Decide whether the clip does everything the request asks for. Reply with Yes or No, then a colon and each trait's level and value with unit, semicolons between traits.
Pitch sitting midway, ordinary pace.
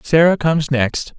Yes: medium, 150 Hz; average, 150 wpm